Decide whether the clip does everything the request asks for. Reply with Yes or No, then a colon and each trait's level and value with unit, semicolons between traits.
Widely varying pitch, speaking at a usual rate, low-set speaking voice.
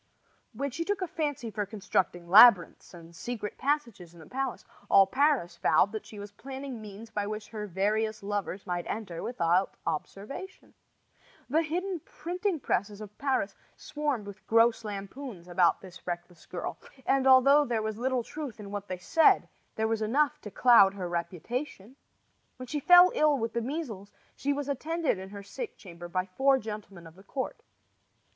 No: wide, 6.1 semitones; average, 175 wpm; high, 220 Hz